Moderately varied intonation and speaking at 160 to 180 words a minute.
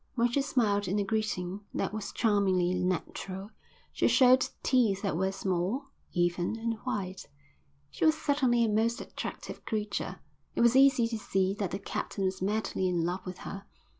Yes: average, 3.9 semitones; average, 170 wpm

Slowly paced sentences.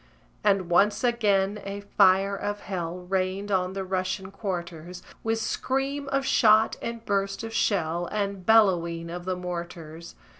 No: average, 145 wpm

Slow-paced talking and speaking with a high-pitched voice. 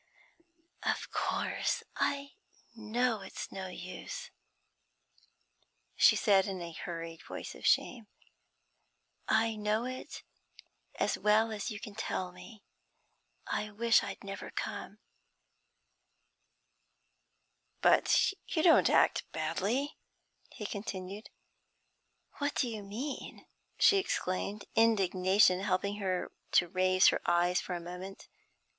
Yes: slow, 110 wpm; high, 200 Hz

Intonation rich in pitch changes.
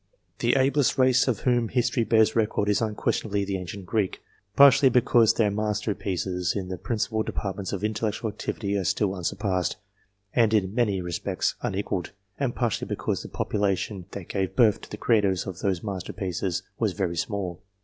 No: average, 3.2 semitones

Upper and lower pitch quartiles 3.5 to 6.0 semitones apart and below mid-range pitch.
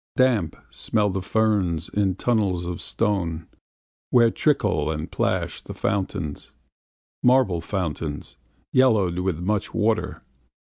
Yes: average, 4.4 semitones; very low, 95 Hz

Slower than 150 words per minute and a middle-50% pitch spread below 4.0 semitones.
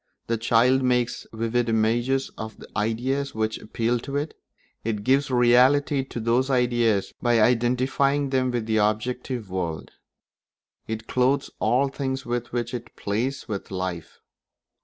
Yes: average, 140 wpm; average, 2.9 semitones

